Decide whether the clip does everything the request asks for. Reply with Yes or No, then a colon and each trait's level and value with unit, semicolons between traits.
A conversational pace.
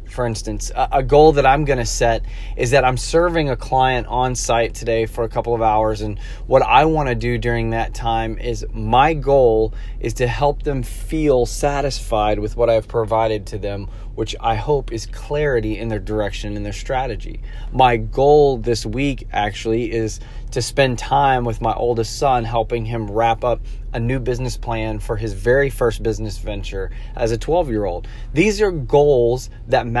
Yes: average, 190 wpm